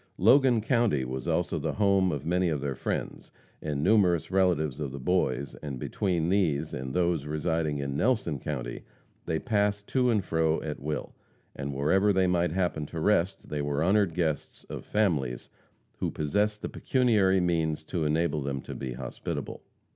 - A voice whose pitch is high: No, very low, 80 Hz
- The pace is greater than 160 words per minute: Yes, average, 170 wpm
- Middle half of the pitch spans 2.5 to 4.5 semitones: No, average, 5.0 semitones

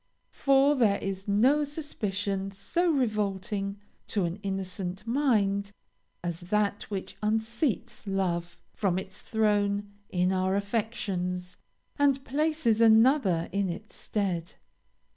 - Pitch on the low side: No, high, 205 Hz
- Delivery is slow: Yes, slow, 110 wpm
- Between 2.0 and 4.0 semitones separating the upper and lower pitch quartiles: Yes, average, 3.3 semitones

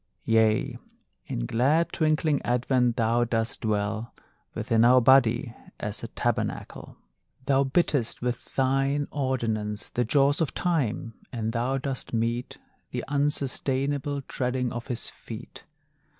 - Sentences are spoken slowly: Yes, slow, 120 wpm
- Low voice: Yes, low, 125 Hz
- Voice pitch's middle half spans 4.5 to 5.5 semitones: No, average, 3.3 semitones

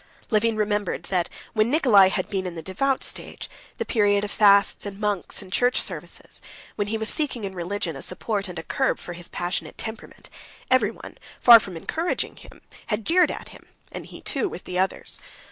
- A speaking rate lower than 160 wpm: No, average, 195 wpm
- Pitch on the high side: Yes, high, 205 Hz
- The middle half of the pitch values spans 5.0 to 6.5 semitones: No, average, 3.3 semitones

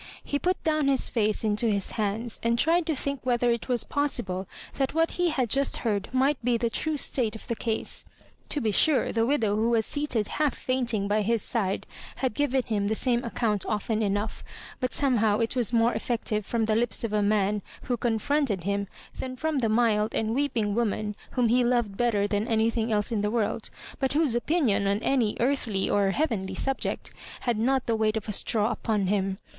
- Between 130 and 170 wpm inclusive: No, fast, 205 wpm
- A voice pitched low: No, high, 230 Hz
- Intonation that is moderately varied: Yes, average, 3.5 semitones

